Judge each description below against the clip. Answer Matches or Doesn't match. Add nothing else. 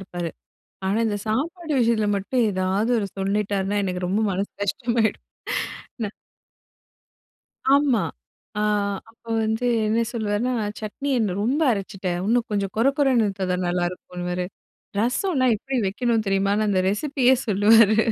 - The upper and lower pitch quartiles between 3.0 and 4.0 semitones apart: Matches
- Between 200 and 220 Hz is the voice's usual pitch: Matches